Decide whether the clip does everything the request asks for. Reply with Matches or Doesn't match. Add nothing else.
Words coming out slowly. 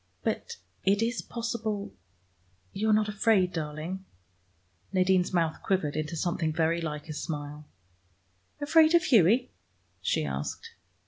Matches